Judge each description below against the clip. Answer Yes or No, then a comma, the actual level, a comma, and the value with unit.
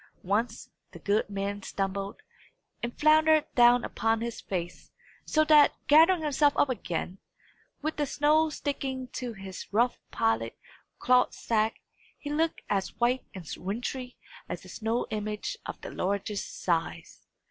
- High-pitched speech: Yes, high, 240 Hz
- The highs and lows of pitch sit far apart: Yes, wide, 6.4 semitones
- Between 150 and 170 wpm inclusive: No, average, 140 wpm